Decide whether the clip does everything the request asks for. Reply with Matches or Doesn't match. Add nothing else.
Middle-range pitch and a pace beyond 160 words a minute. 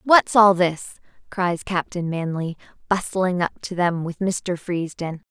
Doesn't match